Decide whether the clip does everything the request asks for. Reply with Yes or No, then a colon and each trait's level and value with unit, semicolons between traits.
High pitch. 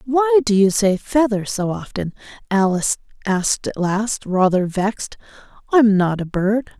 Yes: high, 210 Hz